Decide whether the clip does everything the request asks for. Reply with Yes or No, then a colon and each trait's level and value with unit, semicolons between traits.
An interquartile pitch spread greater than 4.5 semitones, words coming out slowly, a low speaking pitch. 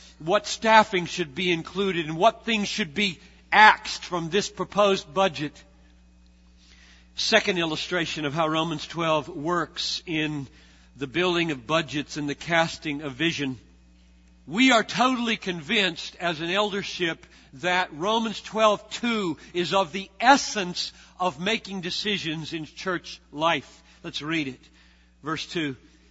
No: average, 5.1 semitones; slow, 130 wpm; medium, 170 Hz